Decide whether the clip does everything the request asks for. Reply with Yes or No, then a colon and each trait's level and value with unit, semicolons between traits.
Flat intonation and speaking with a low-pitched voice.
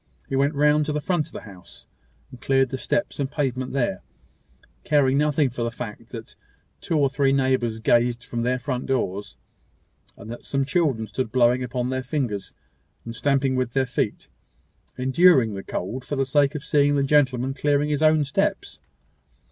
No: average, 3.1 semitones; low, 130 Hz